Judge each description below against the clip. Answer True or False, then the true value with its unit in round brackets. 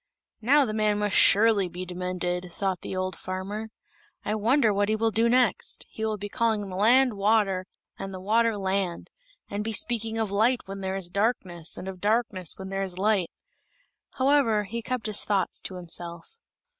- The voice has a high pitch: True (205 Hz)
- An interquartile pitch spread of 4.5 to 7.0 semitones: False (3.1 semitones)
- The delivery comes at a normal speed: True (185 wpm)